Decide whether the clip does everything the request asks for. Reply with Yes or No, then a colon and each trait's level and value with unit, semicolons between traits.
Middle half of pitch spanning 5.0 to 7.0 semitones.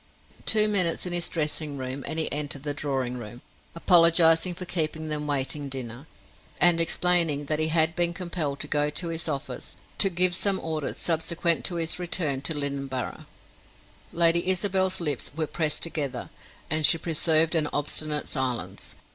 No: average, 3.0 semitones